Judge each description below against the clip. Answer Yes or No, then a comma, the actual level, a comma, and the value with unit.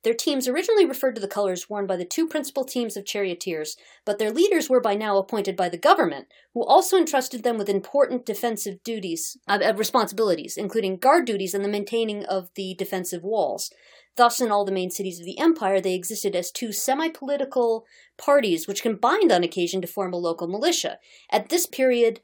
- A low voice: No, high, 220 Hz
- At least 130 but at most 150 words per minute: No, average, 195 wpm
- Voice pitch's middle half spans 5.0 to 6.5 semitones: Yes, average, 5.3 semitones